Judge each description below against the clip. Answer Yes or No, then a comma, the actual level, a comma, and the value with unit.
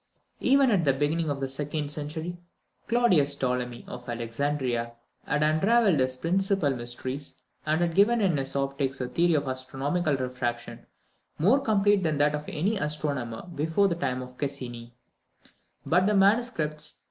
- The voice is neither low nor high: Yes, medium, 150 Hz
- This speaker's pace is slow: No, average, 150 wpm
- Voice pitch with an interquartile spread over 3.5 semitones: Yes, average, 5.2 semitones